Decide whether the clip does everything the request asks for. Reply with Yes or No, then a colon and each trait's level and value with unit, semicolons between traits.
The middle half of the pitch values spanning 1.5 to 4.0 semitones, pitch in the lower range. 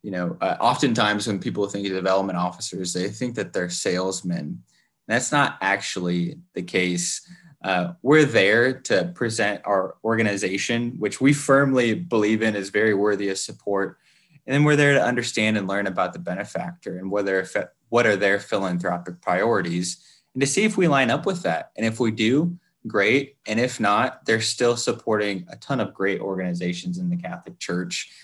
No: average, 5.3 semitones; low, 105 Hz